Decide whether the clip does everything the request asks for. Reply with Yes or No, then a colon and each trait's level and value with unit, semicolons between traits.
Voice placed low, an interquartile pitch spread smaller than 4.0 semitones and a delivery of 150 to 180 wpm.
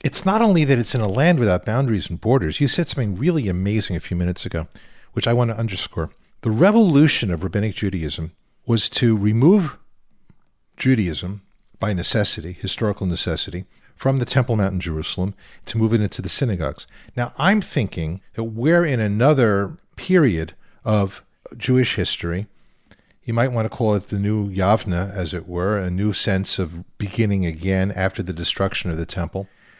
No: low, 105 Hz; average, 4.7 semitones; average, 175 wpm